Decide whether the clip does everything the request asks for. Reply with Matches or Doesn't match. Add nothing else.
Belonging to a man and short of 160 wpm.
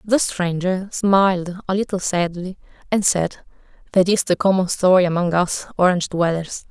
Doesn't match